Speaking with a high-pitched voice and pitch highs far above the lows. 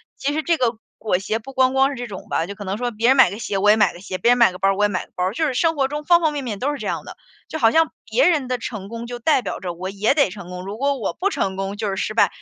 Yes: high, 230 Hz; wide, 5.7 semitones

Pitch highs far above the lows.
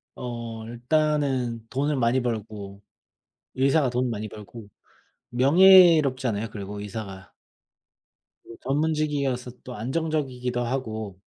No: average, 4.0 semitones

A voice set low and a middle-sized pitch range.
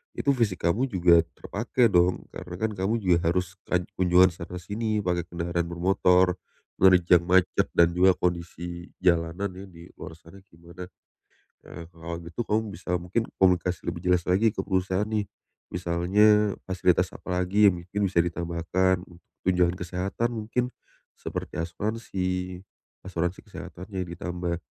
No: very low, 90 Hz; narrow, 2.1 semitones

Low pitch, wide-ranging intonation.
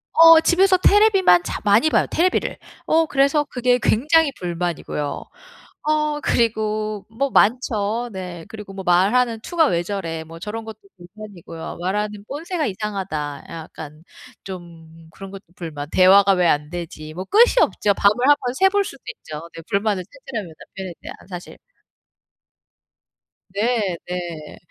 No: high, 200 Hz; wide, 6.4 semitones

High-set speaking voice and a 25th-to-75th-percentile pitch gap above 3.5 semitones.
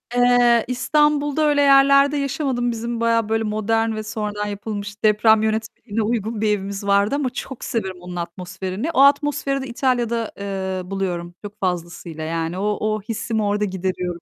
Yes: high, 215 Hz; average, 3.9 semitones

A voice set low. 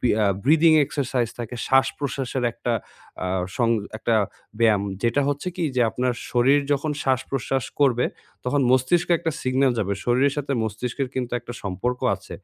Yes: low, 130 Hz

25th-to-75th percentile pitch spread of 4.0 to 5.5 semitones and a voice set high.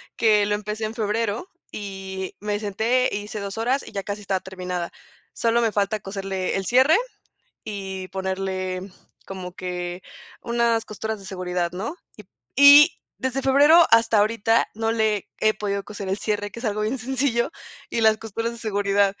No: average, 3.0 semitones; high, 210 Hz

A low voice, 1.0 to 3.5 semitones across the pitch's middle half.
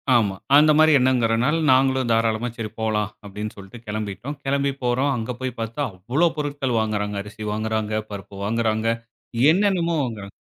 No: low, 115 Hz; average, 4.0 semitones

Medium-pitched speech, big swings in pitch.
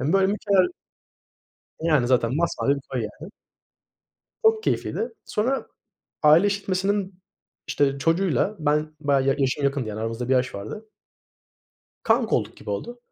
Yes: medium, 155 Hz; wide, 7.2 semitones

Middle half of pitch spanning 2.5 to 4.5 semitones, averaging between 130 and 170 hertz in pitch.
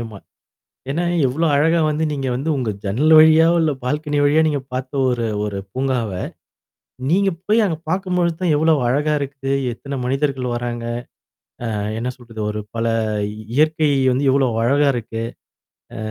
Yes: average, 4.1 semitones; medium, 140 Hz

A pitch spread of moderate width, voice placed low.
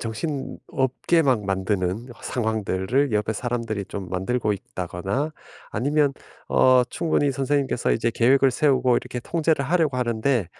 Yes: average, 4.8 semitones; low, 125 Hz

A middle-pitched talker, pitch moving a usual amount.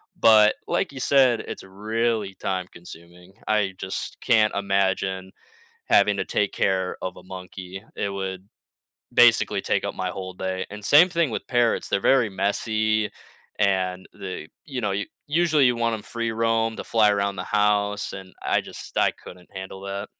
No: low, 100 Hz; average, 3.0 semitones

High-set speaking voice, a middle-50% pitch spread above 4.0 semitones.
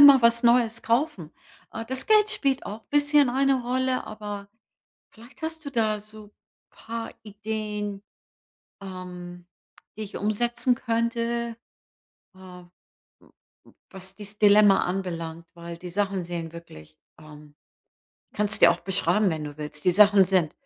Yes: high, 210 Hz; average, 4.6 semitones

